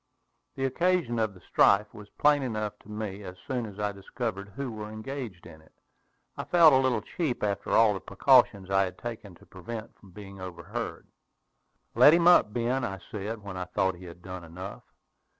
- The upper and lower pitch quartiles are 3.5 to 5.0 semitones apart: Yes, average, 3.9 semitones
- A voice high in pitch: No, low, 105 Hz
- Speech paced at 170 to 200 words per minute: Yes, average, 190 wpm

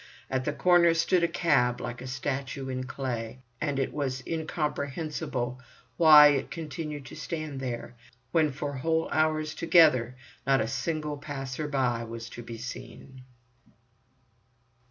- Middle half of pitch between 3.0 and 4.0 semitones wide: Yes, average, 3.3 semitones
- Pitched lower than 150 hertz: Yes, medium, 140 Hz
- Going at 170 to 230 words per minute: No, average, 140 wpm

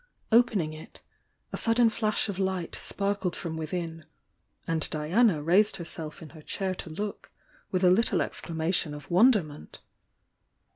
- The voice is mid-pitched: Yes, medium, 180 Hz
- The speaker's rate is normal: Yes, average, 145 wpm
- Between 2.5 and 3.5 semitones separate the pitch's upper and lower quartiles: No, average, 4.2 semitones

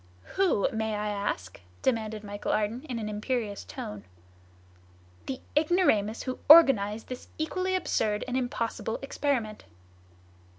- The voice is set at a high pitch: Yes, high, 225 Hz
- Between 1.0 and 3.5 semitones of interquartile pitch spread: No, average, 4.3 semitones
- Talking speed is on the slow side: Yes, slow, 120 wpm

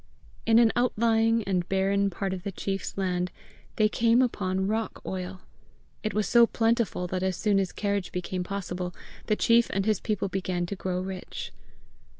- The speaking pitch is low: No, high, 195 Hz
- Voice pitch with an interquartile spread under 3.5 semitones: Yes, average, 3.1 semitones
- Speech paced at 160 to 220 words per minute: Yes, average, 170 wpm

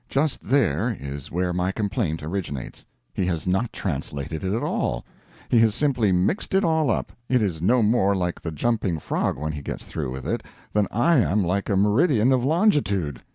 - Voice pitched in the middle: No, low, 100 Hz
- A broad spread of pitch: Yes, wide, 6.4 semitones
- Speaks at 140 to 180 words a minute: No, average, 195 wpm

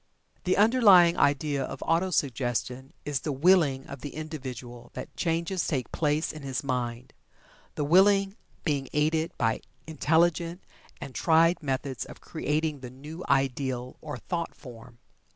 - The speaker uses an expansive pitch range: No, average, 4.1 semitones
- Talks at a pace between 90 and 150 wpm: Yes, average, 145 wpm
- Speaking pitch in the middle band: Yes, medium, 150 Hz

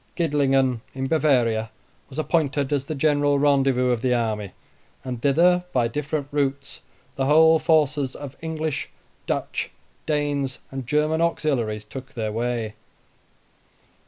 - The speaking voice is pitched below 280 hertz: Yes, medium, 140 Hz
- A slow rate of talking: Yes, slow, 130 wpm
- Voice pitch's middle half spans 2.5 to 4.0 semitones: Yes, average, 3.3 semitones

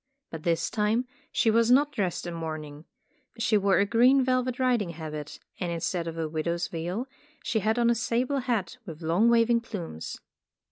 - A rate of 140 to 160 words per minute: No, average, 180 wpm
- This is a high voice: Yes, high, 205 Hz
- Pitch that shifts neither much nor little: No, wide, 6.1 semitones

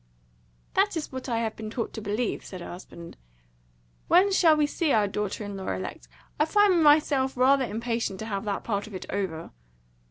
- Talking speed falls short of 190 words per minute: No, average, 195 wpm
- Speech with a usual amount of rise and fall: No, wide, 6.6 semitones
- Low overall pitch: No, high, 230 Hz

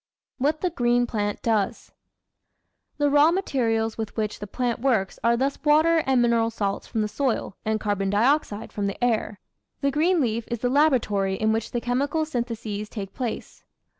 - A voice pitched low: No, high, 235 Hz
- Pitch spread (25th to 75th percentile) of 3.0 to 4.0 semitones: No, average, 4.4 semitones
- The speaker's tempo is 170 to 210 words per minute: Yes, average, 175 wpm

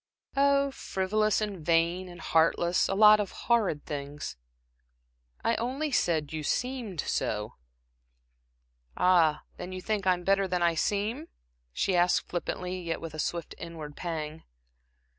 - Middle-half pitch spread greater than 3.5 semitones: Yes, average, 4.3 semitones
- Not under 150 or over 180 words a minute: No, average, 140 wpm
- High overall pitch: No, medium, 180 Hz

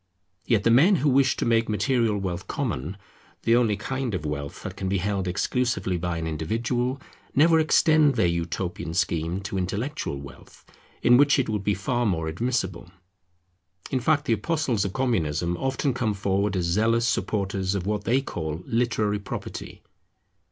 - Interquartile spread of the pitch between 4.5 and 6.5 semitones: Yes, wide, 5.6 semitones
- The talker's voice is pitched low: Yes, low, 105 Hz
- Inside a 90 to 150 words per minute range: No, average, 165 wpm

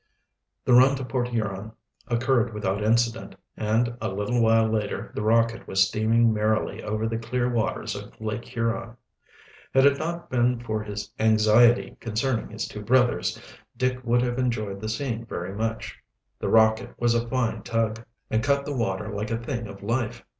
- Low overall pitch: Yes, low, 115 Hz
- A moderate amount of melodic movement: No, narrow, 2.0 semitones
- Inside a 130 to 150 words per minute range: No, average, 175 wpm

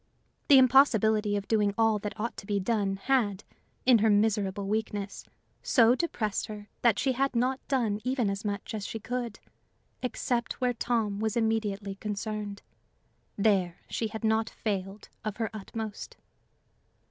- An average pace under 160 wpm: Yes, average, 150 wpm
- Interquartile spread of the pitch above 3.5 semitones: No, narrow, 2.6 semitones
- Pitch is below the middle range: No, high, 215 Hz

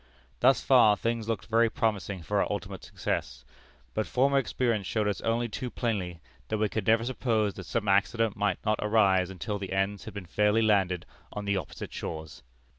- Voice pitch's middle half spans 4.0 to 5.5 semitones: No, average, 2.7 semitones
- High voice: No, low, 105 Hz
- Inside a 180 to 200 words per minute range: Yes, average, 190 wpm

